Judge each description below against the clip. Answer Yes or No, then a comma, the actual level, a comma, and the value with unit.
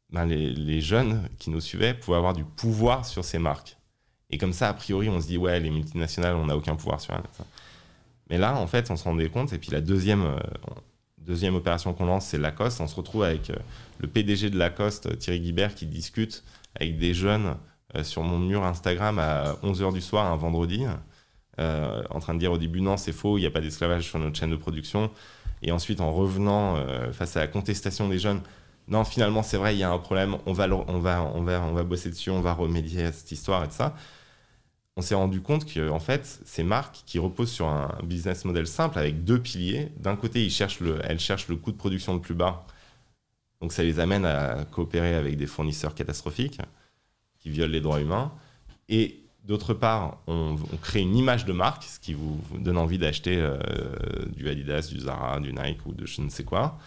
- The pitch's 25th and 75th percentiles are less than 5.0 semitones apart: Yes, average, 4.0 semitones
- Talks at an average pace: No, fast, 225 wpm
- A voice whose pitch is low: Yes, very low, 90 Hz